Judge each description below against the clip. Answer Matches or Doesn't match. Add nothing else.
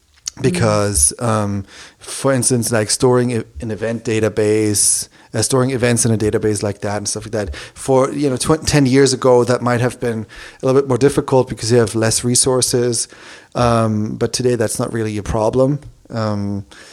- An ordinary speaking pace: Matches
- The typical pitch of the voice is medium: Doesn't match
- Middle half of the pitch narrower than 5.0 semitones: Matches